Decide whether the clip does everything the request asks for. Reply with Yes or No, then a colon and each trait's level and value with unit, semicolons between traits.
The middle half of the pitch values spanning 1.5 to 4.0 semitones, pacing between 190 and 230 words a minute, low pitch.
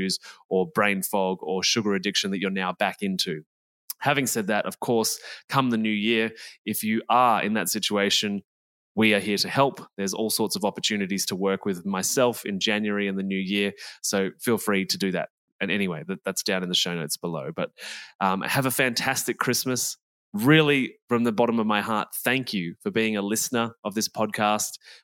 Yes: average, 2.9 semitones; average, 200 wpm; low, 105 Hz